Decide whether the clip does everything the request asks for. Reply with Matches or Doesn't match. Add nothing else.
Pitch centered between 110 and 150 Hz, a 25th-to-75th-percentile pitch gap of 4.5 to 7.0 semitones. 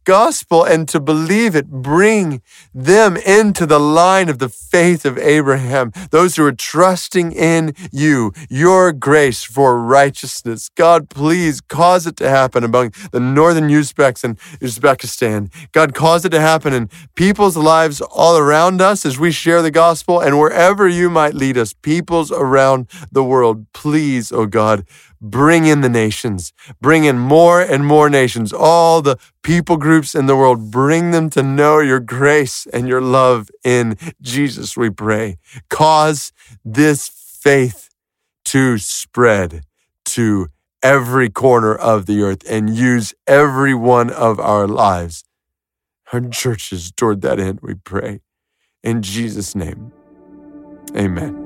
Matches